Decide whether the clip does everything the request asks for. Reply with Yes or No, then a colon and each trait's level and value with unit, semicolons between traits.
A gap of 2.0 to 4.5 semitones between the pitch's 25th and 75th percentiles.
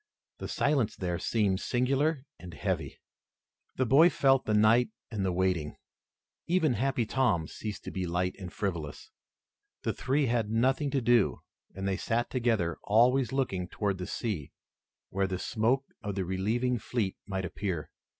No: average, 5.2 semitones